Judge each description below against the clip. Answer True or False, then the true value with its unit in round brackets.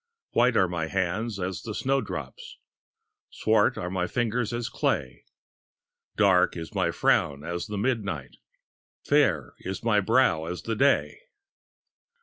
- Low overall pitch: True (100 Hz)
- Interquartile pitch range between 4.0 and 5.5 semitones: True (4.9 semitones)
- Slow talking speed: True (130 wpm)